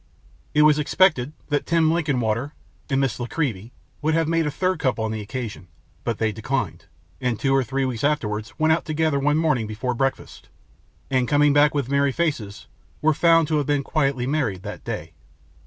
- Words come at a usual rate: Yes, average, 190 wpm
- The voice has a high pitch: No, medium, 140 Hz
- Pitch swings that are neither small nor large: Yes, average, 4.3 semitones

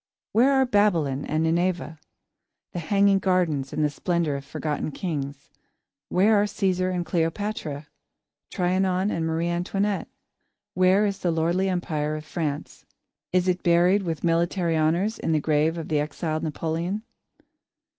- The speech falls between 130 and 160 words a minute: Yes, average, 145 wpm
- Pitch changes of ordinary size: Yes, average, 3.1 semitones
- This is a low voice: No, medium, 170 Hz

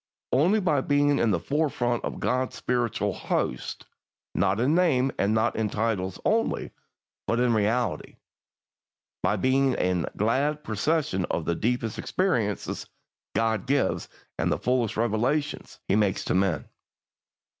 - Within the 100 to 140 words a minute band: Yes, slow, 135 wpm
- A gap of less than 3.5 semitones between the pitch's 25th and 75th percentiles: No, average, 5.0 semitones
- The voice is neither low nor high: No, low, 120 Hz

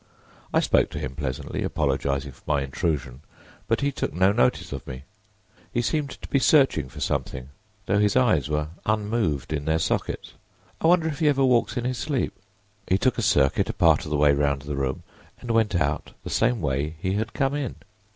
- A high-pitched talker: No, very low, 95 Hz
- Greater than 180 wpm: Yes, fast, 205 wpm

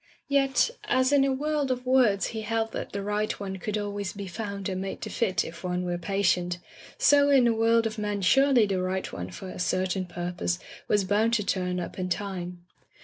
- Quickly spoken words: Yes, fast, 215 wpm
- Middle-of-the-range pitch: No, high, 200 Hz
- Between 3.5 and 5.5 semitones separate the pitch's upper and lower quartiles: Yes, average, 4.0 semitones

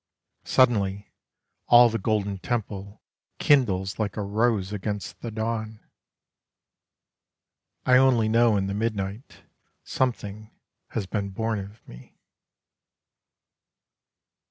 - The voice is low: Yes, low, 110 Hz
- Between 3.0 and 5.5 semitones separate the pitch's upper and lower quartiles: No, narrow, 2.6 semitones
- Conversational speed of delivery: No, slow, 100 wpm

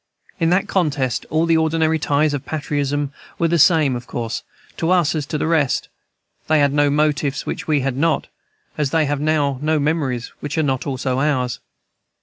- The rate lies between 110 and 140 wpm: No, average, 190 wpm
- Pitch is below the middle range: No, medium, 145 Hz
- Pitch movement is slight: Yes, narrow, 2.3 semitones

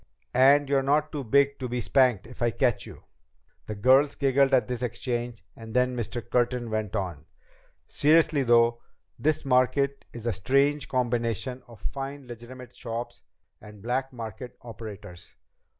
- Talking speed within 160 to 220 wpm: No, average, 150 wpm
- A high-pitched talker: No, low, 125 Hz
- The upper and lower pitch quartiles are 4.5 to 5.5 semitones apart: No, average, 2.8 semitones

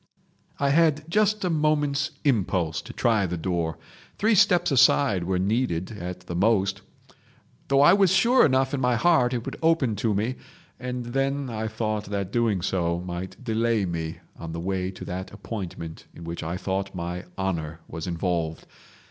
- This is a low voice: Yes, low, 105 Hz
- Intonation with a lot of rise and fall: Yes, wide, 7.2 semitones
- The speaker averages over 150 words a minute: Yes, average, 170 wpm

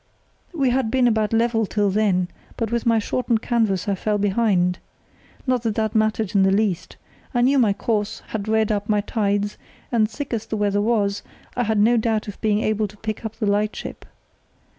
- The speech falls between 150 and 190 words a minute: No, average, 200 wpm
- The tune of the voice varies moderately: No, narrow, 1.9 semitones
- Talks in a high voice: Yes, high, 215 Hz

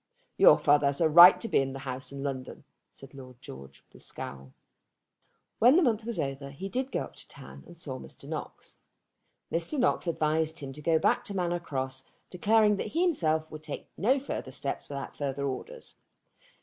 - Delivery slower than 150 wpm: No, average, 200 wpm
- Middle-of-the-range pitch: Yes, medium, 155 Hz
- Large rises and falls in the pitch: Yes, wide, 6.4 semitones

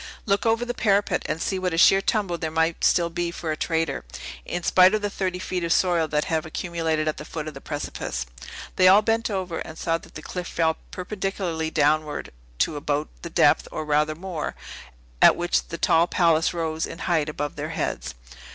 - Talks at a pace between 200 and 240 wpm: Yes, fast, 205 wpm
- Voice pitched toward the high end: No, medium, 165 Hz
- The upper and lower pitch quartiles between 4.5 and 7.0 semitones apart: No, average, 3.0 semitones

